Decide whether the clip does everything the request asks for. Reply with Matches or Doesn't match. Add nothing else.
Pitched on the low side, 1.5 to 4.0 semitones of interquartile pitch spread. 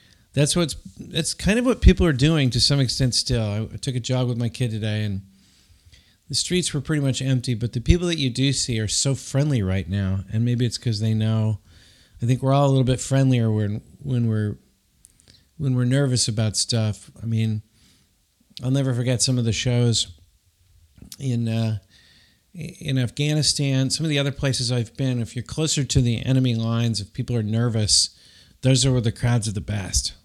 Matches